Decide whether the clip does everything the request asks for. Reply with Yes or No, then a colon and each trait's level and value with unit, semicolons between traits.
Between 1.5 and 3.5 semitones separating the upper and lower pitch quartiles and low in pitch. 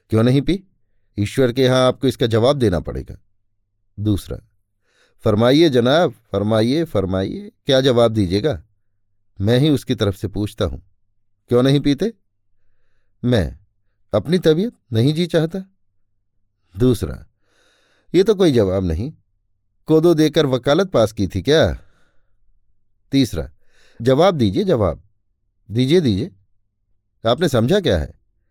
No: average, 4.5 semitones; low, 105 Hz